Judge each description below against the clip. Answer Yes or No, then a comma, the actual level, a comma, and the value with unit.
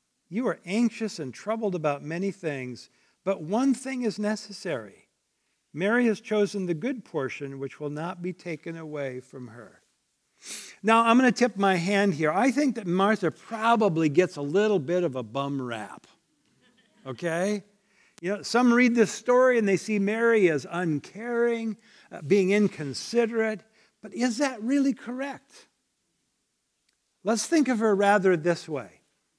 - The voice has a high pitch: Yes, high, 200 Hz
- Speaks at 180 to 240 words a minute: No, average, 155 wpm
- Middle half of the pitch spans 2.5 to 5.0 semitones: No, wide, 5.6 semitones